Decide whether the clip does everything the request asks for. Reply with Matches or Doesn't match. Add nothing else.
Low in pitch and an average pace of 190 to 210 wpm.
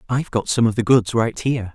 Doesn't match